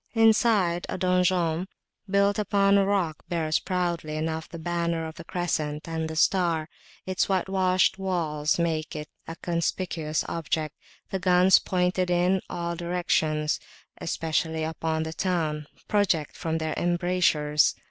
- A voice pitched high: No, medium, 170 Hz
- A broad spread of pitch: No, narrow, 2.5 semitones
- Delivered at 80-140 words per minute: Yes, slow, 135 wpm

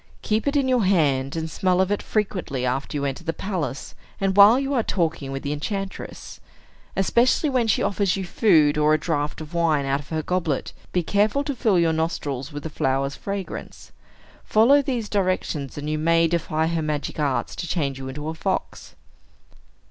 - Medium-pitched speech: Yes, medium, 165 Hz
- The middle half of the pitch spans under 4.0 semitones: No, wide, 5.4 semitones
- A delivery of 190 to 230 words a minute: Yes, average, 195 wpm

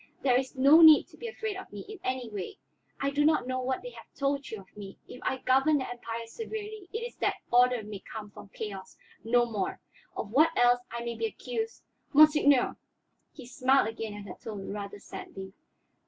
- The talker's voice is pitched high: Yes, very high, 255 Hz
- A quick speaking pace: Yes, fast, 210 wpm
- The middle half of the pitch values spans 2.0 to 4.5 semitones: No, wide, 5.5 semitones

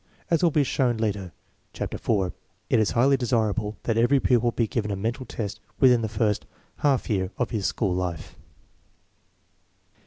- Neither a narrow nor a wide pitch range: Yes, average, 3.2 semitones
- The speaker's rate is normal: Yes, average, 165 wpm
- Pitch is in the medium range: No, low, 115 Hz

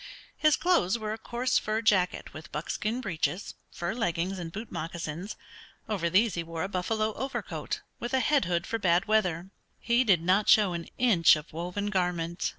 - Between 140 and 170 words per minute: No, average, 180 wpm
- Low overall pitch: No, high, 190 Hz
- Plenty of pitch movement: No, average, 4.3 semitones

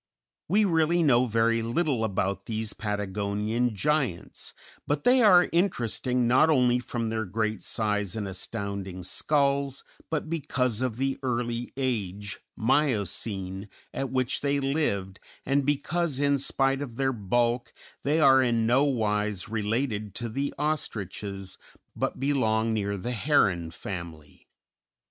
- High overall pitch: No, low, 120 Hz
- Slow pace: Yes, slow, 130 wpm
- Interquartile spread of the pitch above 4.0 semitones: Yes, average, 5.1 semitones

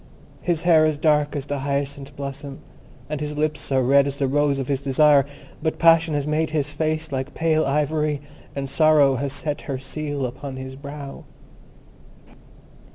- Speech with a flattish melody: Yes, narrow, 1.8 semitones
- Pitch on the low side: No, medium, 145 Hz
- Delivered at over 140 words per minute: Yes, average, 170 wpm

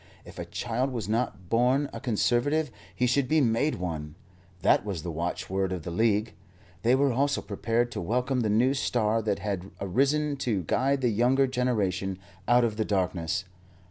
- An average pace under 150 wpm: No, average, 175 wpm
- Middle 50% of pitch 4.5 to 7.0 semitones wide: Yes, average, 4.9 semitones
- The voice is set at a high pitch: No, low, 115 Hz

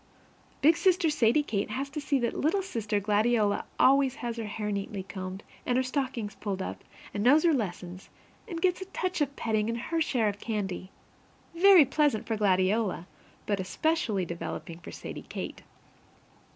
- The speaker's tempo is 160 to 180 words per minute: Yes, average, 170 wpm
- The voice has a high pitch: Yes, high, 230 Hz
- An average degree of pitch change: No, wide, 6.4 semitones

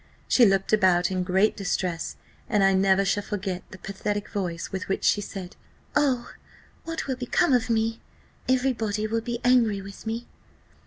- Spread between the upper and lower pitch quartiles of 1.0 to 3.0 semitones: No, average, 3.6 semitones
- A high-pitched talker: Yes, high, 205 Hz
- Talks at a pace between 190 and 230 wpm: No, average, 170 wpm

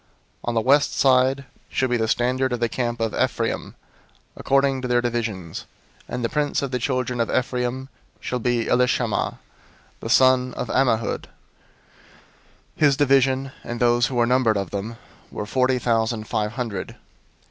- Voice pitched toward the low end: Yes, low, 125 Hz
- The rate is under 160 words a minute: No, average, 165 wpm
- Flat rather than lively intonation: Yes, narrow, 2.1 semitones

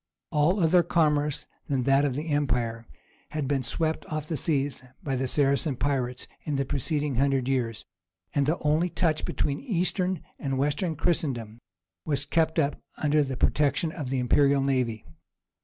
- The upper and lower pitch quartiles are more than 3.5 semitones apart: No, average, 2.8 semitones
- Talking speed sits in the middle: Yes, average, 160 wpm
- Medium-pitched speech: Yes, medium, 145 Hz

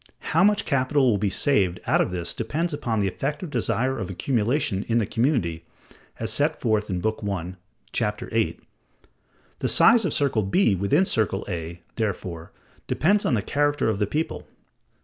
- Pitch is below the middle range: Yes, low, 115 Hz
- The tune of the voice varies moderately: No, wide, 6.8 semitones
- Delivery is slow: No, average, 170 wpm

